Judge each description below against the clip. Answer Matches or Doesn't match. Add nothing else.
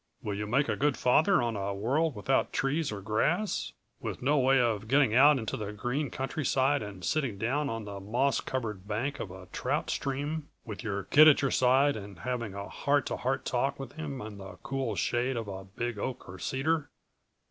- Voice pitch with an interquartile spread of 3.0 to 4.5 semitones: Doesn't match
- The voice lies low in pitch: Matches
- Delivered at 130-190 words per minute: Doesn't match